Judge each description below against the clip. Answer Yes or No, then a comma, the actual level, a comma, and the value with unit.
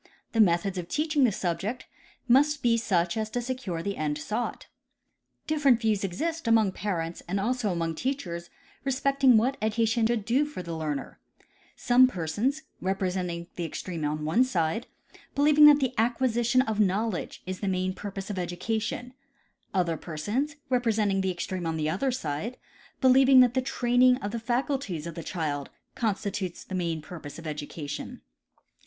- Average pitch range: No, wide, 6.5 semitones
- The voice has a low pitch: No, high, 210 Hz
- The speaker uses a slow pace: No, average, 165 wpm